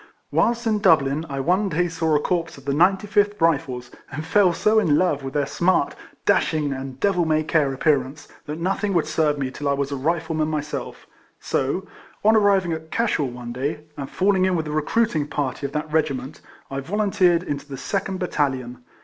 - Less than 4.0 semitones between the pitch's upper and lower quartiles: No, average, 4.7 semitones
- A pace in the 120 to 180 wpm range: No, average, 200 wpm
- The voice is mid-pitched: Yes, medium, 155 Hz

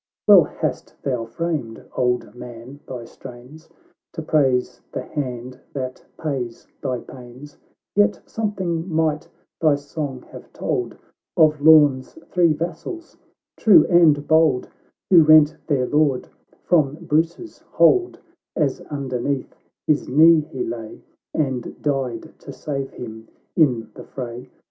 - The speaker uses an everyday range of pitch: Yes, average, 4.1 semitones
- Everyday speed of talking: No, slow, 130 wpm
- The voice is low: No, medium, 145 Hz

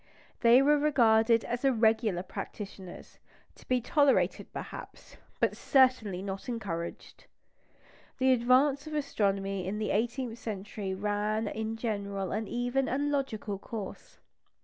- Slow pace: Yes, slow, 125 wpm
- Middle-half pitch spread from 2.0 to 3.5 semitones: No, average, 4.2 semitones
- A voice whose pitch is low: No, high, 225 Hz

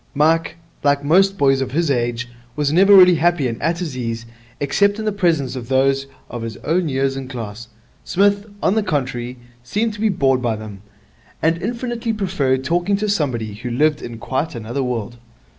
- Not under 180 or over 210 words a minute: Yes, average, 190 wpm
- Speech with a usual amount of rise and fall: No, wide, 6.6 semitones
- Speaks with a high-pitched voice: No, medium, 140 Hz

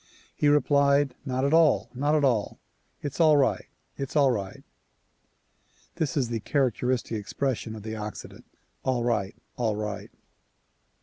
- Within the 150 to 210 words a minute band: No, average, 140 wpm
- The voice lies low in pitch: Yes, low, 130 Hz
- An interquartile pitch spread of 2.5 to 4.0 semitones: No, average, 4.5 semitones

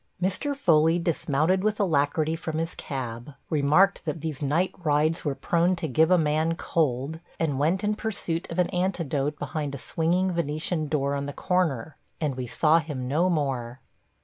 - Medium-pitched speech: Yes, medium, 160 Hz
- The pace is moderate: Yes, average, 175 wpm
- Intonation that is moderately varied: Yes, average, 3.4 semitones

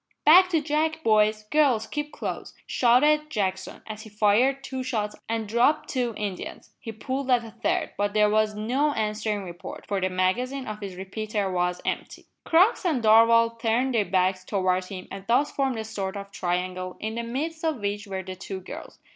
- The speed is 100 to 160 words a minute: No, average, 190 wpm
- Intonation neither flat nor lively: Yes, average, 4.7 semitones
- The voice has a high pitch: Yes, high, 220 Hz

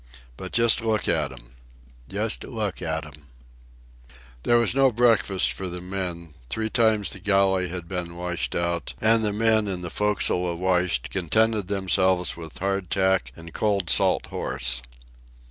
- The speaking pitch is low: Yes, very low, 95 Hz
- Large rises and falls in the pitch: No, average, 3.6 semitones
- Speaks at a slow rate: No, average, 155 wpm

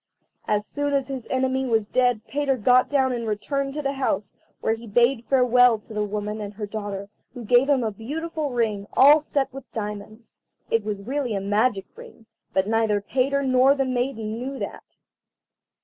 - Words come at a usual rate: Yes, average, 190 wpm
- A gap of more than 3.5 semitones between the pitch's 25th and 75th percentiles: Yes, average, 4.3 semitones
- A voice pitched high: Yes, high, 245 Hz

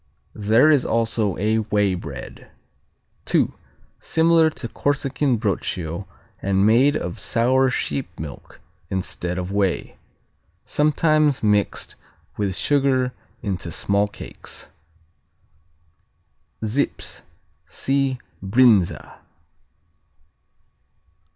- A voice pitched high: No, low, 110 Hz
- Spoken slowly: Yes, slow, 85 wpm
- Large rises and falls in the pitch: Yes, wide, 5.8 semitones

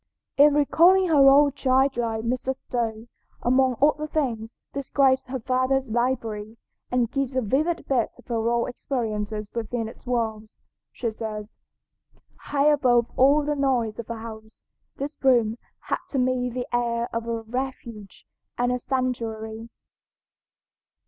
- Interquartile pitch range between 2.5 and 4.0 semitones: Yes, average, 3.1 semitones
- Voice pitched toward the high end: Yes, high, 245 Hz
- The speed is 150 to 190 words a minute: No, average, 140 wpm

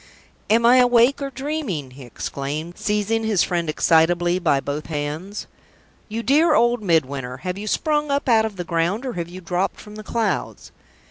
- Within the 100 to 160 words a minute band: No, average, 180 wpm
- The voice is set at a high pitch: Yes, high, 195 Hz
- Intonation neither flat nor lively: No, wide, 6.3 semitones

